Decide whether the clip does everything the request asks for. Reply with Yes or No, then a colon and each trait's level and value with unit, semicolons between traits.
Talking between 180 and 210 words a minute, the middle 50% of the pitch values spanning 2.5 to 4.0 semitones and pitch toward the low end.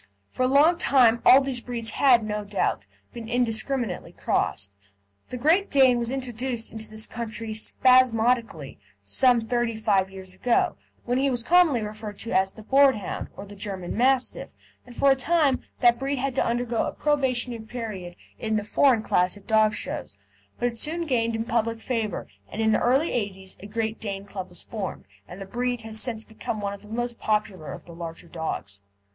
No: average, 190 wpm; average, 3.3 semitones; high, 230 Hz